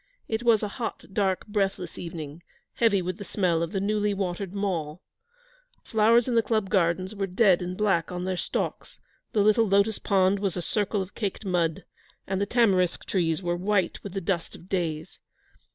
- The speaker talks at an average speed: Yes, average, 190 wpm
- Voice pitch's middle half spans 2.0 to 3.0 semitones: Yes, average, 2.7 semitones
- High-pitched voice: Yes, high, 195 Hz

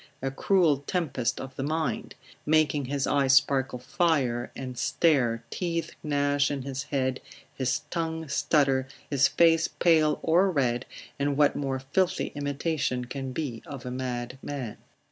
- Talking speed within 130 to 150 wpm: Yes, average, 145 wpm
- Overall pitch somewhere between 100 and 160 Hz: Yes, medium, 140 Hz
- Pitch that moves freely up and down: No, average, 3.1 semitones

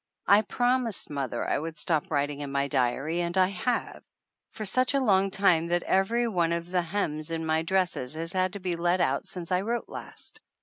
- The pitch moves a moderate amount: Yes, average, 3.6 semitones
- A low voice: No, medium, 175 Hz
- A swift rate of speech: Yes, fast, 210 wpm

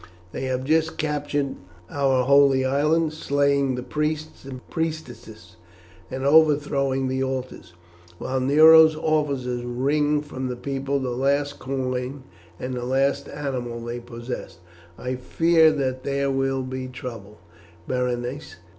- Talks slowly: Yes, slow, 130 wpm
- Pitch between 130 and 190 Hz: Yes, low, 135 Hz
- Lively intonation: No, narrow, 2.4 semitones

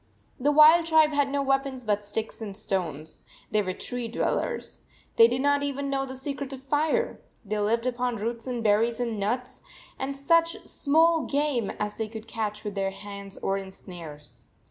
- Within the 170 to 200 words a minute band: Yes, average, 185 wpm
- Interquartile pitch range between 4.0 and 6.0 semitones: Yes, average, 5.2 semitones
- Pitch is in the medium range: No, high, 240 Hz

